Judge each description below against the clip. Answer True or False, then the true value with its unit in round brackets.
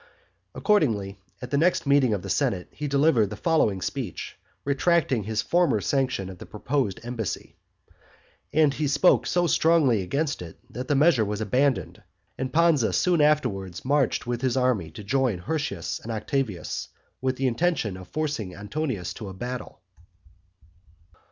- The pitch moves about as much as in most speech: False (6.2 semitones)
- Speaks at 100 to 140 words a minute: False (155 wpm)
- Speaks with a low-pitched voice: True (130 Hz)